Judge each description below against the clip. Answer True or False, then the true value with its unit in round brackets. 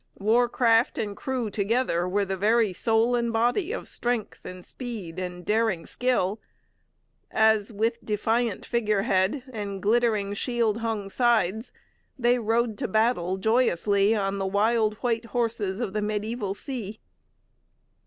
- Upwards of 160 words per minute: False (135 wpm)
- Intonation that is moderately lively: True (3.0 semitones)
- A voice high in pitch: True (220 Hz)